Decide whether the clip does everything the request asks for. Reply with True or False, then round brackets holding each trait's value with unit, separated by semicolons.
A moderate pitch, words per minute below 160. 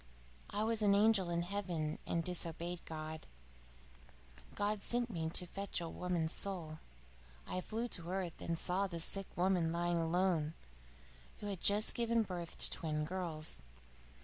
True (180 Hz; 150 wpm)